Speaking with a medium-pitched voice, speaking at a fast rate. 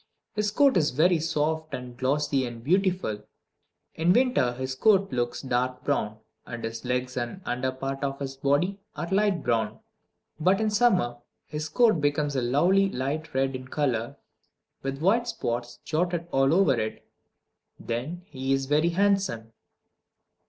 No: medium, 145 Hz; average, 155 wpm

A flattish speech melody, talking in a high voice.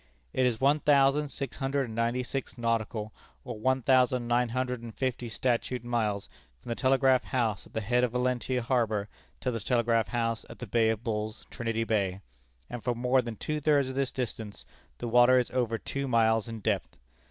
No: narrow, 2.3 semitones; low, 120 Hz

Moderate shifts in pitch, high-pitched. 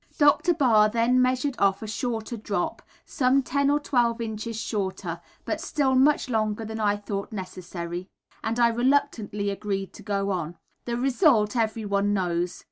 Yes: average, 4.0 semitones; high, 220 Hz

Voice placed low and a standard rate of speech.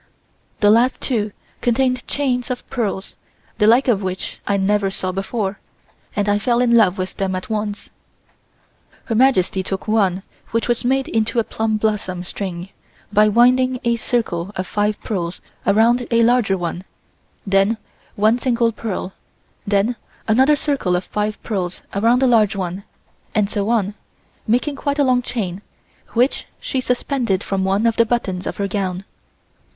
No: high, 215 Hz; average, 160 wpm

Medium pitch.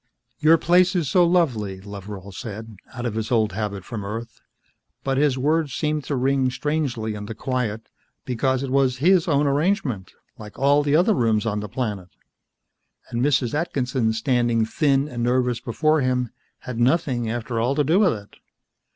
No: low, 125 Hz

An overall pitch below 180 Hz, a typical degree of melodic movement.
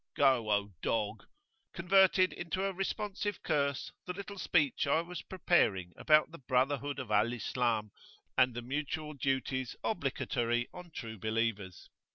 No: low, 135 Hz; wide, 6.9 semitones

